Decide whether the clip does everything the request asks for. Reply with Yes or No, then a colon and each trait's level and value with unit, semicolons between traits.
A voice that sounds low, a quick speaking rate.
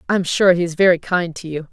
No: medium, 175 Hz; fast, 315 wpm